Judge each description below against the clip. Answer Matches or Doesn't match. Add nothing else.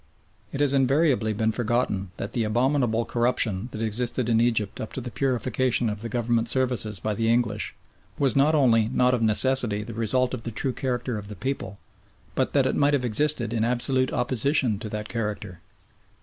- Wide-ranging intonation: Doesn't match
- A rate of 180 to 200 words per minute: Matches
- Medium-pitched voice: Doesn't match